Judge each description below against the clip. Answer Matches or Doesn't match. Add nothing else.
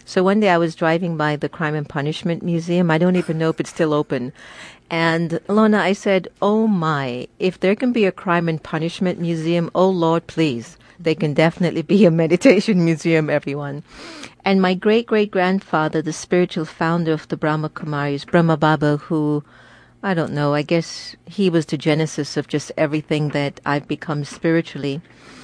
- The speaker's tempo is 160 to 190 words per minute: Matches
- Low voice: Doesn't match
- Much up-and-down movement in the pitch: Doesn't match